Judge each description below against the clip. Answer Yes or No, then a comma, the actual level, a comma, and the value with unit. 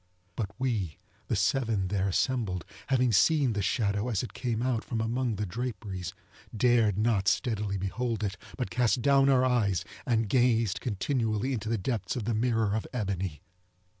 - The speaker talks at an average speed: Yes, average, 165 wpm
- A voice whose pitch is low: Yes, low, 110 Hz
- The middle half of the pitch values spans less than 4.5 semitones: Yes, average, 3.7 semitones